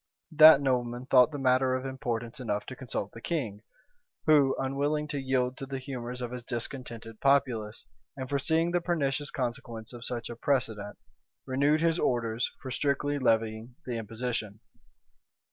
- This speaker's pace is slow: No, average, 155 wpm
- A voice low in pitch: Yes, low, 130 Hz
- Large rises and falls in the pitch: No, average, 3.1 semitones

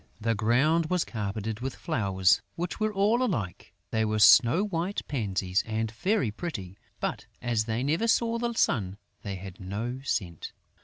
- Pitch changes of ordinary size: No, wide, 8.8 semitones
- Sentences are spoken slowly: No, average, 160 wpm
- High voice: No, low, 115 Hz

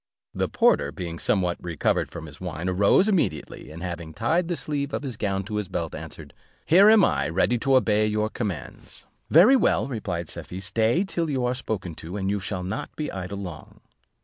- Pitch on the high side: No, low, 105 Hz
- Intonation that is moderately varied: No, wide, 7.3 semitones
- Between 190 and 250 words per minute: Yes, average, 200 wpm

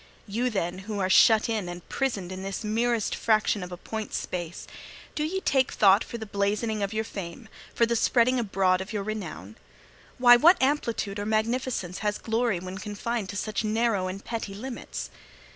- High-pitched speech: Yes, high, 215 Hz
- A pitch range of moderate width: Yes, average, 3.2 semitones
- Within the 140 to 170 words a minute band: No, average, 185 wpm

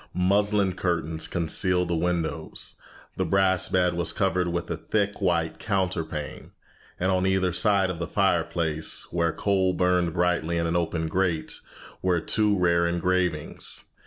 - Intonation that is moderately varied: No, narrow, 2.0 semitones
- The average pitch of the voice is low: Yes, very low, 90 Hz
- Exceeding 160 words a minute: No, average, 145 wpm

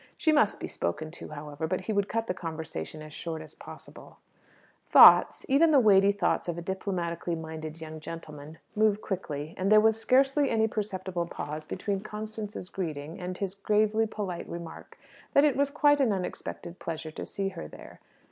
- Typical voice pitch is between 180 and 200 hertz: Yes, medium, 185 Hz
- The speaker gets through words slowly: No, average, 180 wpm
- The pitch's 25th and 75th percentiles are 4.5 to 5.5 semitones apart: Yes, average, 5.1 semitones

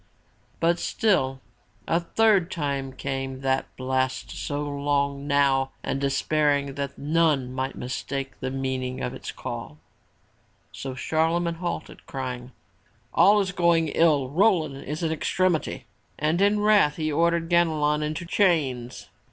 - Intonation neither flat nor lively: Yes, average, 4.0 semitones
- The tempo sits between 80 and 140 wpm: Yes, slow, 135 wpm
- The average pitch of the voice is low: No, medium, 145 Hz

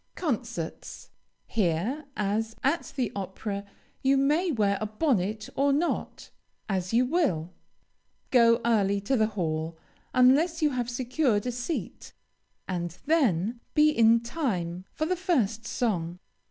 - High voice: Yes, high, 230 Hz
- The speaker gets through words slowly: Yes, slow, 130 wpm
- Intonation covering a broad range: Yes, wide, 5.7 semitones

